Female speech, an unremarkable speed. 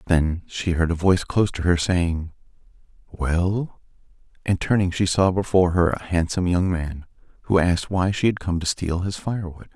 No: male; average, 185 wpm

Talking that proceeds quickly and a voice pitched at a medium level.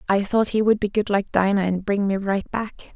No: fast, 265 wpm; high, 200 Hz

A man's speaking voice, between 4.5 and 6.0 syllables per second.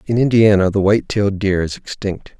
Yes: male; 5.7 syllables/s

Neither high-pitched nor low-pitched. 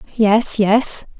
No: high, 215 Hz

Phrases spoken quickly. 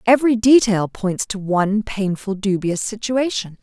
No: slow, 135 wpm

